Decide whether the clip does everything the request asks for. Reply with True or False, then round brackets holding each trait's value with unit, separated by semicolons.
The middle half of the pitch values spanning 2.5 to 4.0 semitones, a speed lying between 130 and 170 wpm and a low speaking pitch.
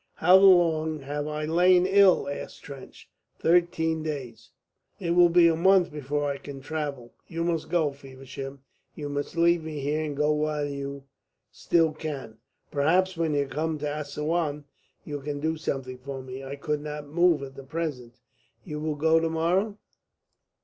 False (2.8 semitones; 165 wpm; 150 Hz)